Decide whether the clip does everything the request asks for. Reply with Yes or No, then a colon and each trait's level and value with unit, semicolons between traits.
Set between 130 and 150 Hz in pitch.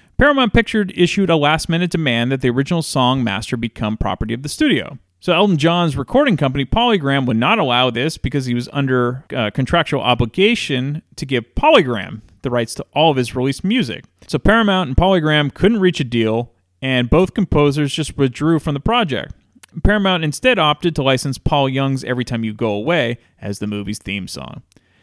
Yes: medium, 140 Hz